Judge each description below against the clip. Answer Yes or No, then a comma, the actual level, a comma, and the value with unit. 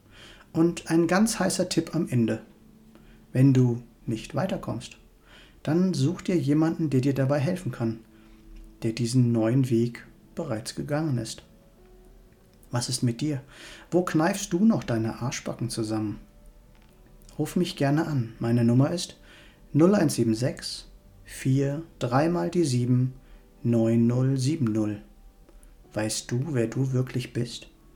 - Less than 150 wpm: Yes, slow, 125 wpm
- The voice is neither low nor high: No, low, 125 Hz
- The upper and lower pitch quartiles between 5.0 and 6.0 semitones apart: Yes, wide, 5.5 semitones